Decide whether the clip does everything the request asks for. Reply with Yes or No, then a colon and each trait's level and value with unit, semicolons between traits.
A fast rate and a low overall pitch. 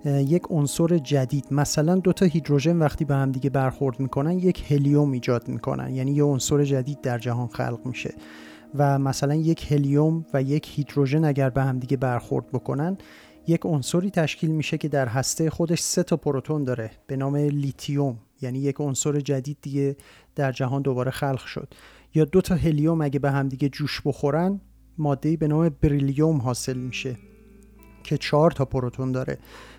No: fast, 160 wpm; medium, 145 Hz